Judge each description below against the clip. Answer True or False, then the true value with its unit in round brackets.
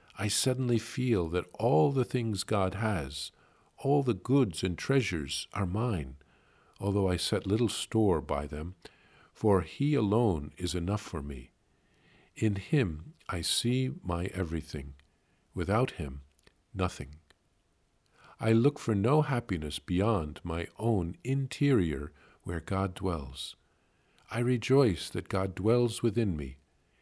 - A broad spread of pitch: True (6.9 semitones)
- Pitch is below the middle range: True (95 Hz)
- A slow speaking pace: True (130 wpm)